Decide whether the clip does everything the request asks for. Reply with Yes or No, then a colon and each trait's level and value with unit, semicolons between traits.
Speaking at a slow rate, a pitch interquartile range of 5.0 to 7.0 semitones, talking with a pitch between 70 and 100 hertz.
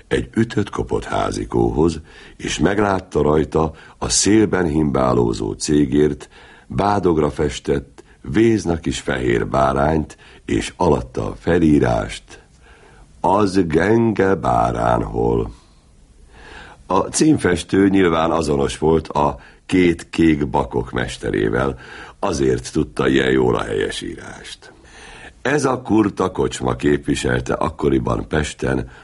Yes: slow, 100 wpm; wide, 5.4 semitones; very low, 80 Hz